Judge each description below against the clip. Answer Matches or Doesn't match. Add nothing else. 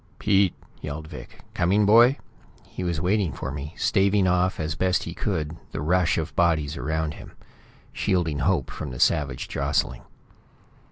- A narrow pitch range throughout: Doesn't match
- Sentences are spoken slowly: Doesn't match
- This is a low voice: Matches